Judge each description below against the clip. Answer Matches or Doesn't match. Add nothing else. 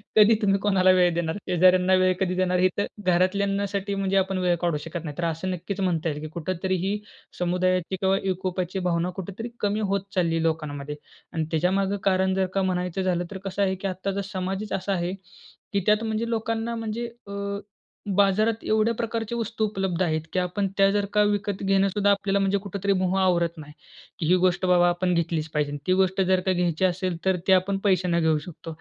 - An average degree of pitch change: Doesn't match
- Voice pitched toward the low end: Doesn't match